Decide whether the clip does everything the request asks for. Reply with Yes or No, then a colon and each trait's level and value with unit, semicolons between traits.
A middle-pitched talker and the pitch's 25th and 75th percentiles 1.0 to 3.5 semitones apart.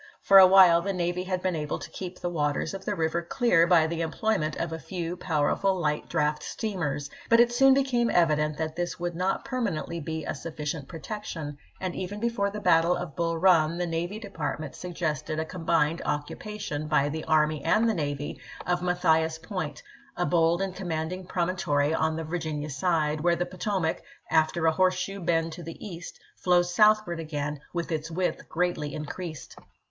Yes: medium, 170 Hz; average, 2.8 semitones